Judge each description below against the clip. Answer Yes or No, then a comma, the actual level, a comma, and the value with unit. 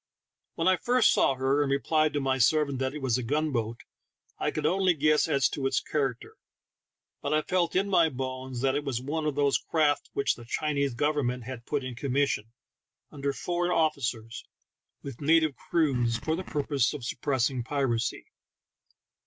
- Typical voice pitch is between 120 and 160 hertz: Yes, medium, 140 Hz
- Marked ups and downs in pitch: No, average, 3.1 semitones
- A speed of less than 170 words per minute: No, average, 175 wpm